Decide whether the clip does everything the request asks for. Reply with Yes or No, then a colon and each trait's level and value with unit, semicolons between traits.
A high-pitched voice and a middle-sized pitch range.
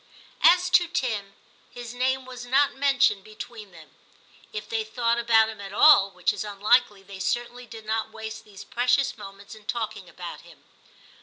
Yes: high, 230 Hz; average, 3.7 semitones